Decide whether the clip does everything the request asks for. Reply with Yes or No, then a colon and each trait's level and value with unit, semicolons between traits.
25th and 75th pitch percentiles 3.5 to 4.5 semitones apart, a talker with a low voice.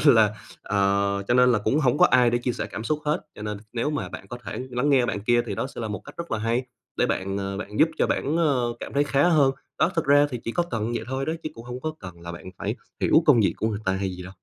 No: average, 5.1 semitones; low, 120 Hz